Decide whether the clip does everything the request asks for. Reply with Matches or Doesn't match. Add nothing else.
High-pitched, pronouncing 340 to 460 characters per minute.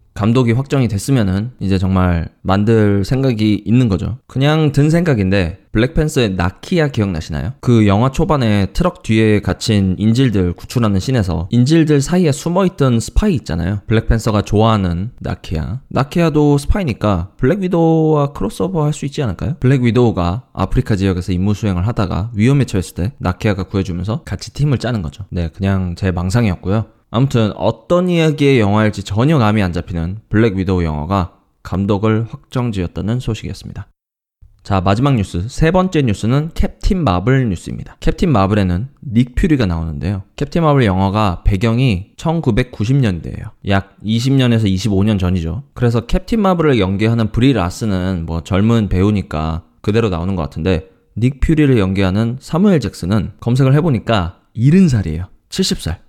Doesn't match